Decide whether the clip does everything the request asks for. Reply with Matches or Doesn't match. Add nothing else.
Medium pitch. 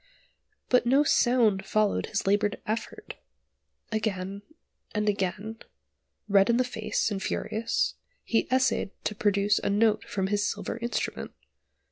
Doesn't match